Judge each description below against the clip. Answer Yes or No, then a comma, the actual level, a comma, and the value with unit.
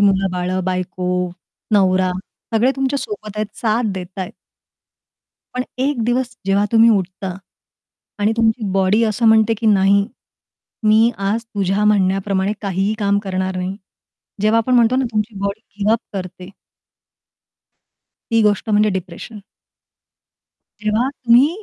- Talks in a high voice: Yes, high, 210 Hz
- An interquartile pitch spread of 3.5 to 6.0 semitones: No, average, 3.1 semitones